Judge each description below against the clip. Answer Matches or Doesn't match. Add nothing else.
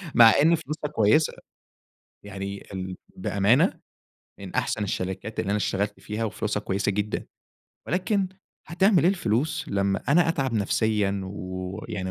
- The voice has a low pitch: Matches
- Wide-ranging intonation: Matches